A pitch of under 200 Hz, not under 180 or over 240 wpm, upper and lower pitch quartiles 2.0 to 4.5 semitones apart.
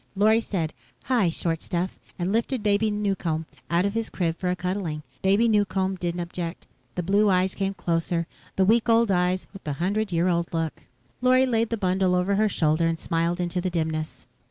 Yes: medium, 185 Hz; average, 200 wpm; average, 3.4 semitones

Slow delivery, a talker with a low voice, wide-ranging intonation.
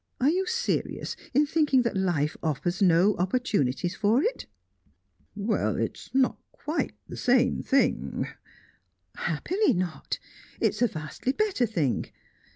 No: slow, 130 wpm; high, 230 Hz; wide, 7.9 semitones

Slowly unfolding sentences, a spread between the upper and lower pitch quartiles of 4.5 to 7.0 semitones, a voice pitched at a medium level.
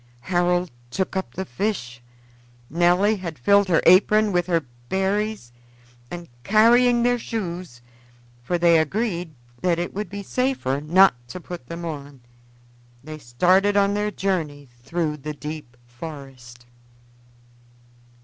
Yes: slow, 130 wpm; average, 5.0 semitones; medium, 175 Hz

